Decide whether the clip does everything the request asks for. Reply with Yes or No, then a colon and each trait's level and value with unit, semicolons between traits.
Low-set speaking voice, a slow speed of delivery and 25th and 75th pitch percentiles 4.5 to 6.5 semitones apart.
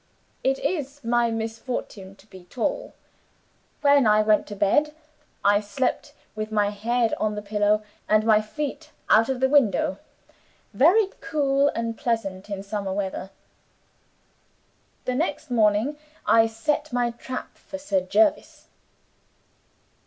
No: high, 225 Hz; slow, 130 wpm; average, 5.0 semitones